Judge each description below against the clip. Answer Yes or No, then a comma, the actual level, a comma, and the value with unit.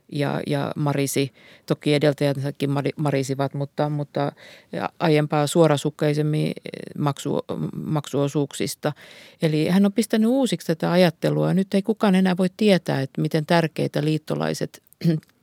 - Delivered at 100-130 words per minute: Yes, average, 115 wpm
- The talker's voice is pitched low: No, medium, 150 Hz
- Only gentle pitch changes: No, average, 4.0 semitones